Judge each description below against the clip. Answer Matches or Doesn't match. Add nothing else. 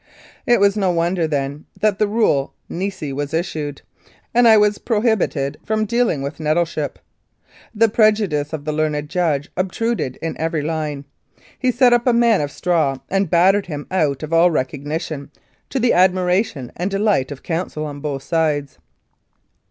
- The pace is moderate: Matches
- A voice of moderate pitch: Matches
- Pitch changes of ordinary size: Doesn't match